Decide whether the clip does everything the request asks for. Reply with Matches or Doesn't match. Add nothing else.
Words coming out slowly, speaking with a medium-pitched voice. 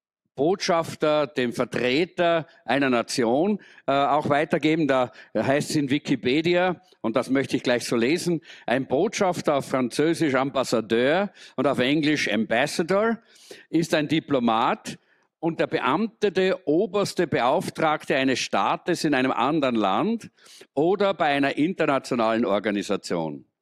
Matches